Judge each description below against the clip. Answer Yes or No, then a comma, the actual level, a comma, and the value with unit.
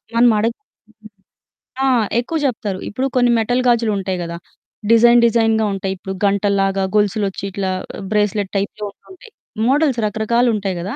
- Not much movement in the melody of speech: No, average, 3.3 semitones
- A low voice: No, high, 215 Hz